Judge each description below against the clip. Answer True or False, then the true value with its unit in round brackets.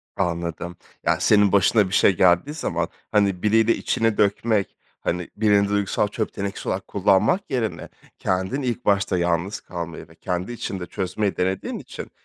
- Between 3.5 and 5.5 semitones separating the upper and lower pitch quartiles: False (2.8 semitones)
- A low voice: True (100 Hz)